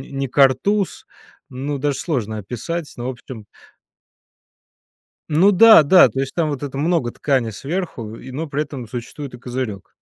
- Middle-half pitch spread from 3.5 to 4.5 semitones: Yes, average, 4.0 semitones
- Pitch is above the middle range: No, low, 135 Hz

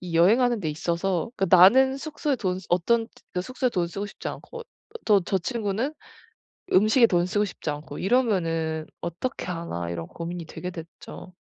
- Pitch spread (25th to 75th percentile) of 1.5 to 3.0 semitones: No, wide, 5.5 semitones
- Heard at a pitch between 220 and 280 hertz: No, medium, 185 Hz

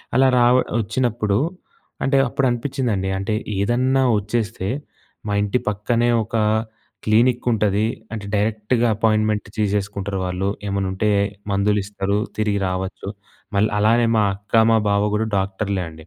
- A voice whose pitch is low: Yes, low, 105 Hz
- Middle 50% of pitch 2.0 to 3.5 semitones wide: Yes, average, 2.7 semitones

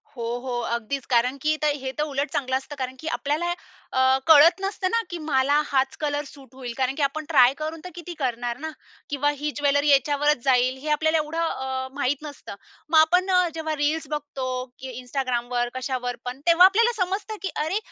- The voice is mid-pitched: No, very high, 285 Hz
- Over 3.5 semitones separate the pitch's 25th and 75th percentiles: No, average, 3.2 semitones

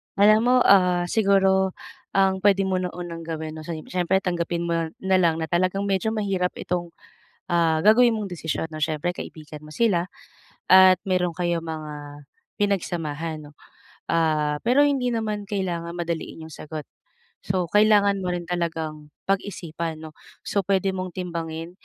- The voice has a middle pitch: Yes, medium, 175 Hz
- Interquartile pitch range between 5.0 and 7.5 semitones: No, average, 3.0 semitones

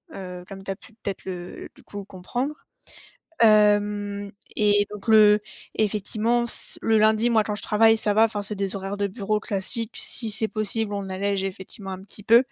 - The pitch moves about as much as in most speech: No, narrow, 1.9 semitones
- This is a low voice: No, high, 205 Hz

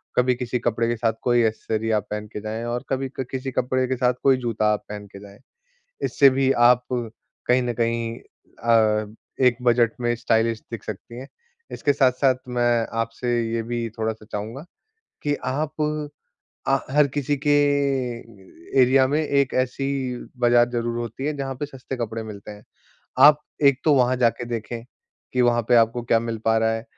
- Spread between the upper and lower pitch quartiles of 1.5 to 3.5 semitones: Yes, narrow, 2.4 semitones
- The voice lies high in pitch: No, low, 120 Hz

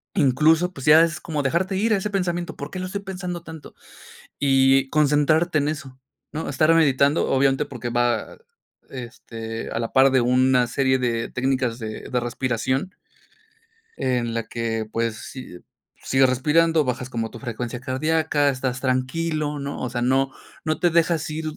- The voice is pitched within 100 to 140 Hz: Yes, low, 135 Hz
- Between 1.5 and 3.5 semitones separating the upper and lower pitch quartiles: No, average, 4.0 semitones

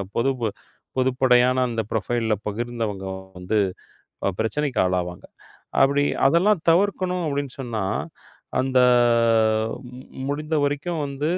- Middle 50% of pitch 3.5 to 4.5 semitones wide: Yes, average, 4.2 semitones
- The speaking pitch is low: Yes, low, 130 Hz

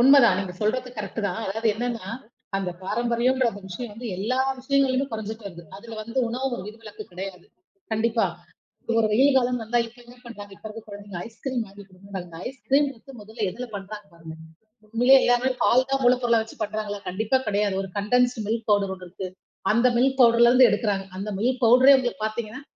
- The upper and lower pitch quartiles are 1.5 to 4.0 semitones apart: Yes, average, 3.4 semitones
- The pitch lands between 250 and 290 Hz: No, high, 225 Hz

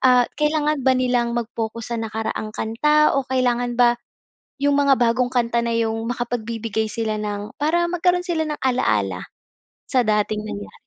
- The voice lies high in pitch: Yes, high, 240 Hz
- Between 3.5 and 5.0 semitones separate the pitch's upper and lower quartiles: No, average, 3.1 semitones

